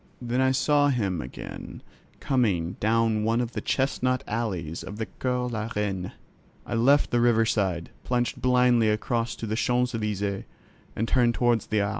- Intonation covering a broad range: No, average, 3.0 semitones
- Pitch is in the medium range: No, low, 115 Hz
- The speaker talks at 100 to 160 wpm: No, average, 170 wpm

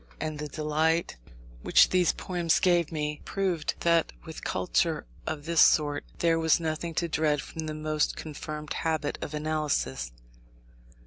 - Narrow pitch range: Yes, narrow, 1.6 semitones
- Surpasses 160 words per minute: No, average, 145 wpm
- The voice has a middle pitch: Yes, medium, 155 Hz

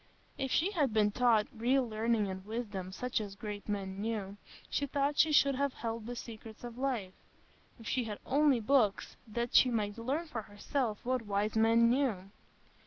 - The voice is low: No, high, 230 Hz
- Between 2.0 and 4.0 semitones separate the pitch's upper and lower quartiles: Yes, average, 3.6 semitones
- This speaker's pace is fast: No, average, 180 wpm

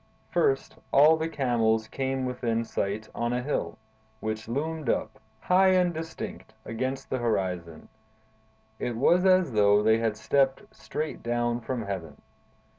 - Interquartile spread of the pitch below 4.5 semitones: No, average, 5.2 semitones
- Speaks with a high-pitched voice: No, low, 120 Hz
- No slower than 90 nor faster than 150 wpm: Yes, average, 140 wpm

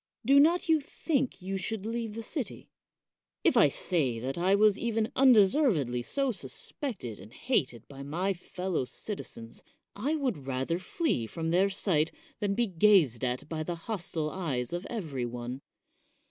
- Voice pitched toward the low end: No, medium, 185 Hz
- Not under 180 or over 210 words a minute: No, average, 160 wpm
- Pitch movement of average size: No, wide, 8.5 semitones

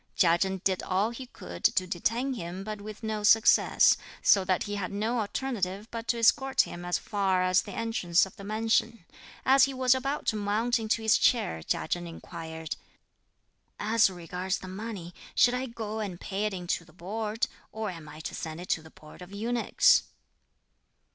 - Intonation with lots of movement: No, average, 4.0 semitones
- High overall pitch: Yes, high, 205 Hz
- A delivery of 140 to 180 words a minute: No, average, 190 wpm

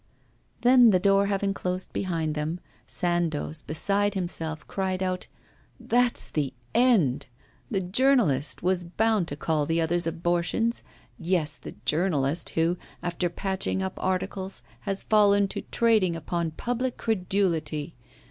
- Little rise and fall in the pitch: No, average, 3.6 semitones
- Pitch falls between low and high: Yes, medium, 180 Hz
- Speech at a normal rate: No, slow, 130 wpm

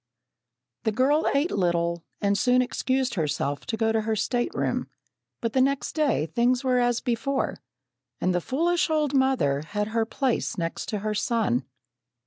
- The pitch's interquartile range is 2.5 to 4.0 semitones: No, average, 4.7 semitones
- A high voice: Yes, high, 235 Hz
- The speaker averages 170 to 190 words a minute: No, average, 160 wpm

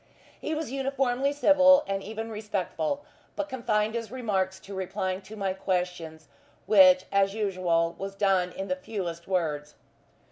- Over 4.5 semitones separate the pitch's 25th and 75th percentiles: No, average, 3.8 semitones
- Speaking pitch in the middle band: No, high, 195 Hz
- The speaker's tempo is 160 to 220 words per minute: No, average, 145 wpm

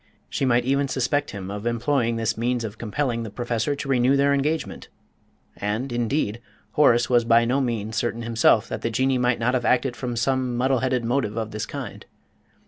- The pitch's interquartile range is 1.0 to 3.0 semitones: Yes, narrow, 2.4 semitones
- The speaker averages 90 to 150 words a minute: No, average, 195 wpm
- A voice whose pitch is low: Yes, low, 120 Hz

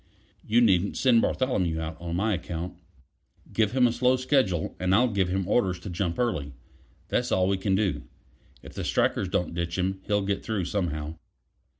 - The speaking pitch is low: Yes, very low, 95 Hz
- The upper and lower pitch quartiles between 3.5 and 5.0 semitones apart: Yes, average, 4.0 semitones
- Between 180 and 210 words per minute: Yes, average, 185 wpm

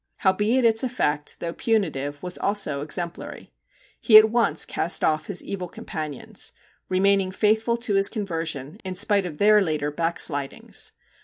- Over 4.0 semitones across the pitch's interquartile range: Yes, wide, 5.4 semitones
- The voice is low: No, medium, 185 Hz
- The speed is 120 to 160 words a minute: Yes, average, 155 wpm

